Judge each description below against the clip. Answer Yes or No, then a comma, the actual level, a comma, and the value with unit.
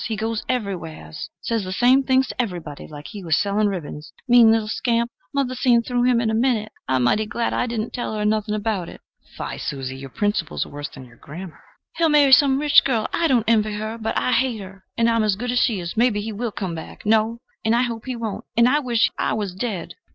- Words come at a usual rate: No, fast, 240 wpm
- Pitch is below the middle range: No, high, 220 Hz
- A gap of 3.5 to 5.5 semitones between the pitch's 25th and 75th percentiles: Yes, average, 3.9 semitones